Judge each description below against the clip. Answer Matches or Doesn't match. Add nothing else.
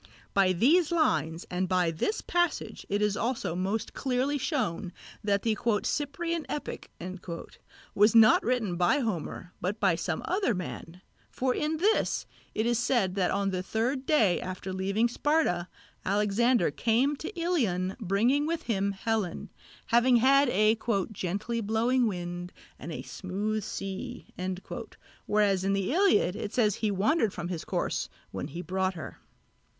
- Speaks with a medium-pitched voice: Doesn't match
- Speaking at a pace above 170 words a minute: Doesn't match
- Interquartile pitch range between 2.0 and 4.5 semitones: Doesn't match